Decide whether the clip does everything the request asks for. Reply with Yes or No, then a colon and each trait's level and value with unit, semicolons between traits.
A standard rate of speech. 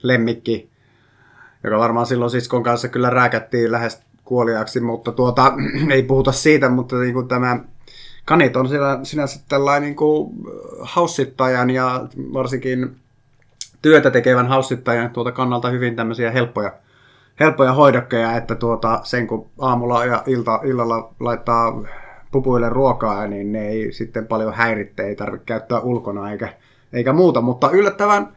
Yes: average, 135 wpm